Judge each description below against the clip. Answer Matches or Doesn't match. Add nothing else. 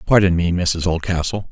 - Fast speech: Doesn't match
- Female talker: Doesn't match